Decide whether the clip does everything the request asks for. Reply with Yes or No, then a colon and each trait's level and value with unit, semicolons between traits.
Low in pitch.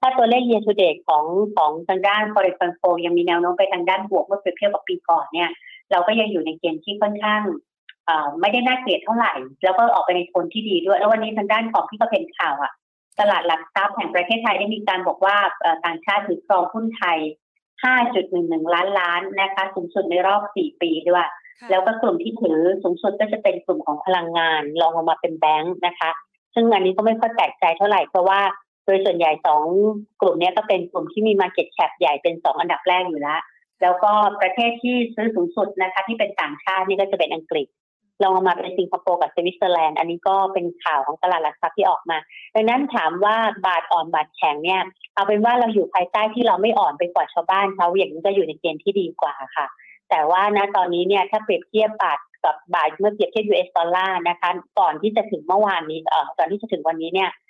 No: high, 190 Hz